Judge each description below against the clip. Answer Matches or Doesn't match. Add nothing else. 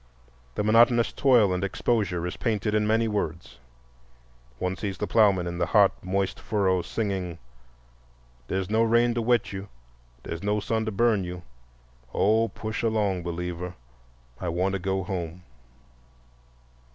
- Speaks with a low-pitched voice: Matches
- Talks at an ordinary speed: Matches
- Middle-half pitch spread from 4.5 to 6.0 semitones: Doesn't match